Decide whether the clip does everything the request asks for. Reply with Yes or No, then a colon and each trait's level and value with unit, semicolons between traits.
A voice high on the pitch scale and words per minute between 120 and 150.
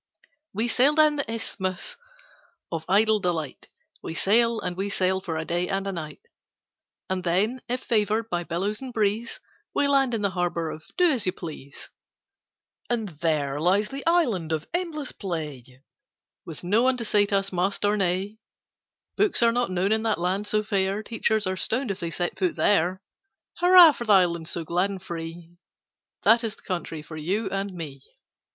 No: high, 195 Hz; average, 185 wpm